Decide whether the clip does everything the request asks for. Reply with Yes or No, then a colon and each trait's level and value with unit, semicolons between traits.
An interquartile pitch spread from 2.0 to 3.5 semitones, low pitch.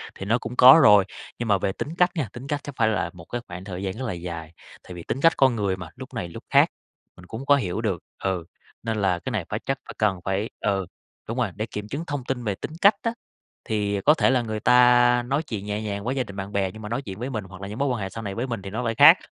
No: average, 4.3 semitones; low, 110 Hz